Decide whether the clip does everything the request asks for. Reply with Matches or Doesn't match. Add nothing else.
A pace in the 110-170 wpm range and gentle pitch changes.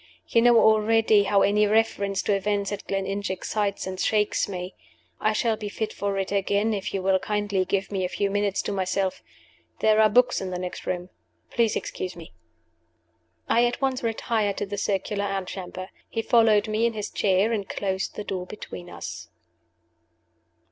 Doesn't match